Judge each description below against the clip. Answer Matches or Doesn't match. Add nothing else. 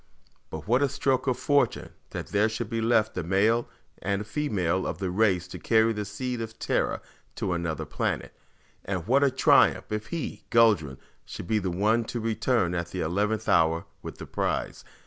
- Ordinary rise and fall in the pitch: Matches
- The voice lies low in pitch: Matches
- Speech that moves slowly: Doesn't match